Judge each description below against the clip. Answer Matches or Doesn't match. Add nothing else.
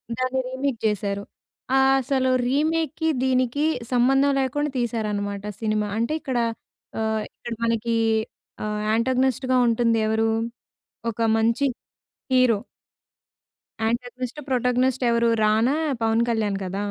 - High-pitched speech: Matches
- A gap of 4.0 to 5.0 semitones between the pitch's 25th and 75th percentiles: Doesn't match